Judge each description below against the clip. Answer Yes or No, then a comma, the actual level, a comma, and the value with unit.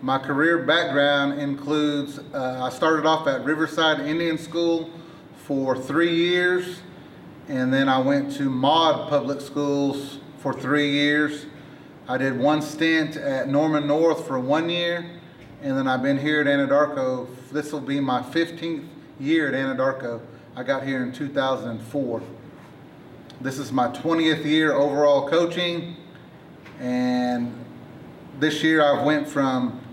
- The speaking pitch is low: No, medium, 145 Hz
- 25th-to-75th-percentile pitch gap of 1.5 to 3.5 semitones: Yes, average, 3.0 semitones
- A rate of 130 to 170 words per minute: Yes, slow, 135 wpm